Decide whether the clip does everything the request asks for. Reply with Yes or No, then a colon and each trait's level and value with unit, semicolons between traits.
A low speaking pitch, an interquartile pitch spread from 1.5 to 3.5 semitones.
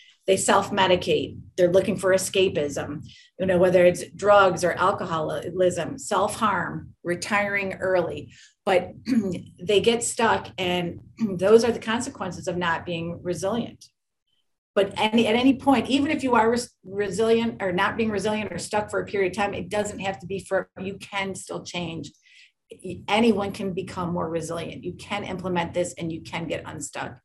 No: high, 195 Hz; average, 2.9 semitones